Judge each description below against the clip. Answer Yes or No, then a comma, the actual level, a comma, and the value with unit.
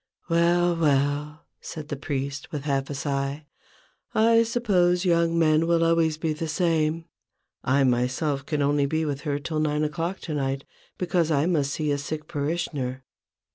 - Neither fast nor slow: Yes, average, 175 wpm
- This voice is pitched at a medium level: Yes, medium, 155 Hz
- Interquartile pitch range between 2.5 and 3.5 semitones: Yes, average, 2.8 semitones